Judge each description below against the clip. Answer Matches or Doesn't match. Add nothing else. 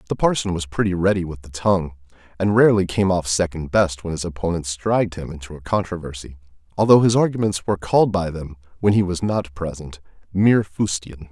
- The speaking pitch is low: Matches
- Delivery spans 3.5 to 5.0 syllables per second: Doesn't match